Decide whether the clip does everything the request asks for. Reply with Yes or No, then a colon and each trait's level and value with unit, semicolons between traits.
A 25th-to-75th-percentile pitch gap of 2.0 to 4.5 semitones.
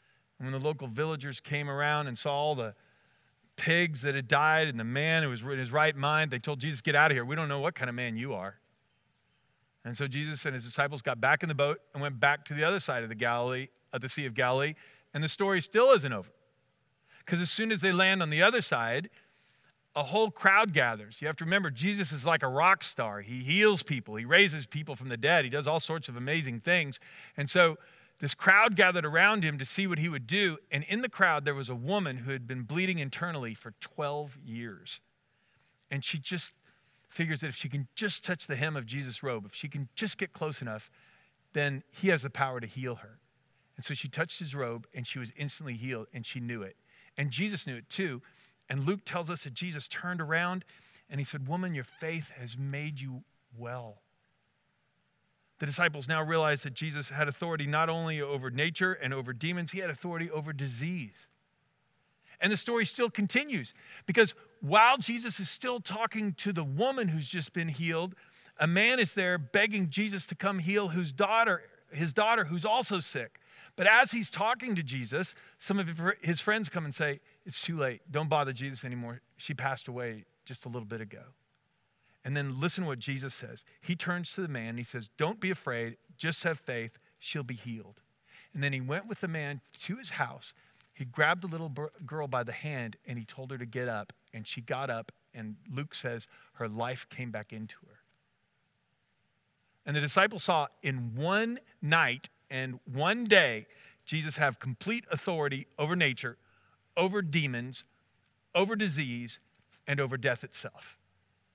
No: average, 5.1 semitones